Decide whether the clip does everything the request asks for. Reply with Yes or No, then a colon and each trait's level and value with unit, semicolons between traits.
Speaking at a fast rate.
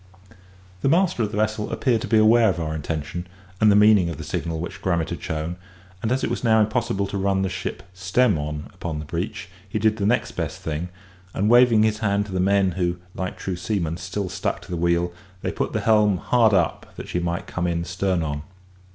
Yes: fast, 230 wpm